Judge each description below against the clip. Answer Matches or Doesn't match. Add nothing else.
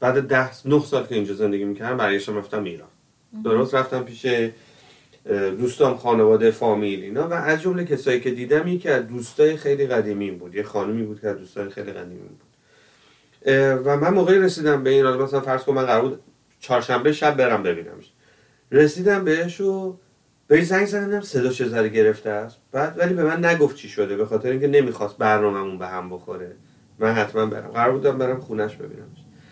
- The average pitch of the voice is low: Matches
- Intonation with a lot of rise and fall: Matches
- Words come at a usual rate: Doesn't match